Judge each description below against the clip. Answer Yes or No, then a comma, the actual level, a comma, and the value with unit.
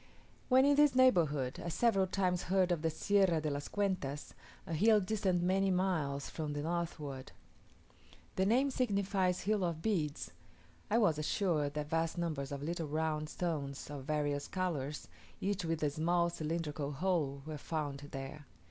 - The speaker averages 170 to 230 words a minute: No, average, 160 wpm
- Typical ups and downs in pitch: Yes, average, 4.4 semitones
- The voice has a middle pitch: Yes, medium, 165 Hz